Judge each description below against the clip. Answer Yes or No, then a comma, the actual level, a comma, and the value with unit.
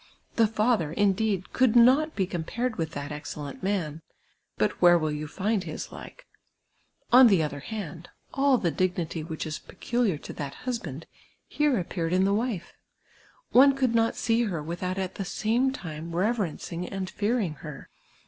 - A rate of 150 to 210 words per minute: Yes, average, 170 wpm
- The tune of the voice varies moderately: No, wide, 5.8 semitones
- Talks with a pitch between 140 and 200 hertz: Yes, high, 190 Hz